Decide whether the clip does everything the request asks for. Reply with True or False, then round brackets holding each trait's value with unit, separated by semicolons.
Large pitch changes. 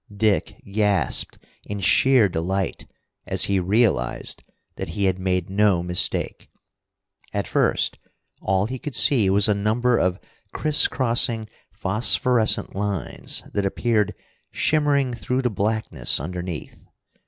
False (3.9 semitones)